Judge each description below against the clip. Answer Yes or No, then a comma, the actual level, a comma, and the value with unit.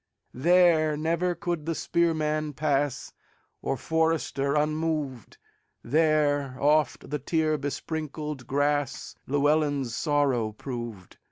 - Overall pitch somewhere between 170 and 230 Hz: No, medium, 150 Hz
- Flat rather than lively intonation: Yes, narrow, 2.3 semitones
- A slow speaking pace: Yes, slow, 80 wpm